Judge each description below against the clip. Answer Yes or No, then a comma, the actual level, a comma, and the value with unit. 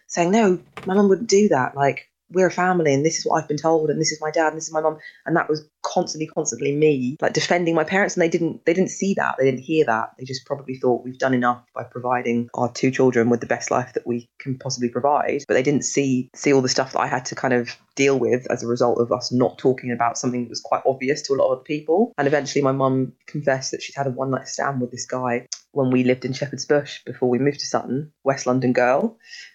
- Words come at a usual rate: No, fast, 270 wpm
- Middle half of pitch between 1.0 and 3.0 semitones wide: No, average, 3.8 semitones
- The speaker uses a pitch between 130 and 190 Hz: Yes, low, 135 Hz